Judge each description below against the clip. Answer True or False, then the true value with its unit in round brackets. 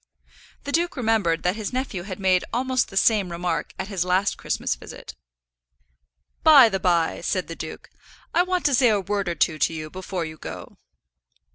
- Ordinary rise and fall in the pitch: False (5.7 semitones)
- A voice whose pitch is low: False (195 Hz)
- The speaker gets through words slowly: False (185 wpm)